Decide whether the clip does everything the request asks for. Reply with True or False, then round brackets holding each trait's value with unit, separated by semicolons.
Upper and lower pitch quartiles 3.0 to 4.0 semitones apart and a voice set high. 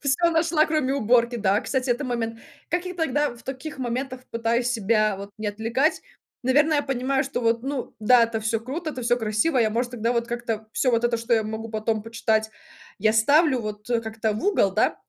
True (3.4 semitones; 240 Hz)